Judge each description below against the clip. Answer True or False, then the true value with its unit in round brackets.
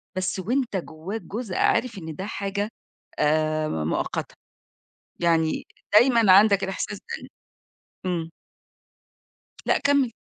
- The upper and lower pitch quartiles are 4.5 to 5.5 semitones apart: True (5.2 semitones)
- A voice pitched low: False (190 Hz)